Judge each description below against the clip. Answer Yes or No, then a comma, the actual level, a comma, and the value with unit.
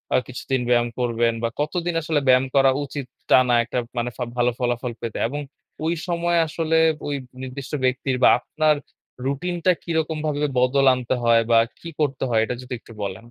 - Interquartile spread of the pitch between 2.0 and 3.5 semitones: No, average, 4.0 semitones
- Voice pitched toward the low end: Yes, low, 130 Hz